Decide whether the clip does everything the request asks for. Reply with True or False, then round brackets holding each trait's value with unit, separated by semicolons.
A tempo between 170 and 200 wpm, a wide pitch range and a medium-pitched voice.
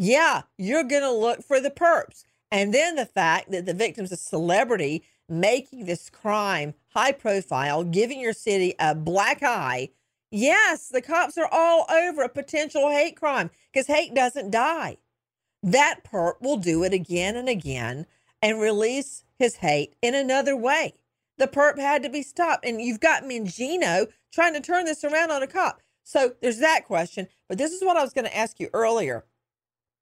False (175 wpm; 7.2 semitones; 245 Hz)